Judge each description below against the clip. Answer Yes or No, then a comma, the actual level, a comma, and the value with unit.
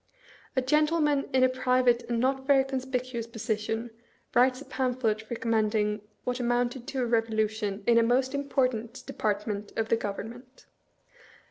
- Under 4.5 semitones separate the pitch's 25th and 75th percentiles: Yes, narrow, 2.6 semitones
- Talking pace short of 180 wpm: Yes, average, 145 wpm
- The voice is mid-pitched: No, high, 240 Hz